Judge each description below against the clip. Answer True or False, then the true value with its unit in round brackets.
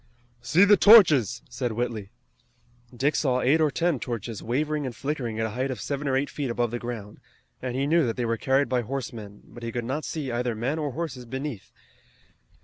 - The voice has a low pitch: True (130 Hz)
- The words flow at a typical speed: False (210 wpm)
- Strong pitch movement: False (3.5 semitones)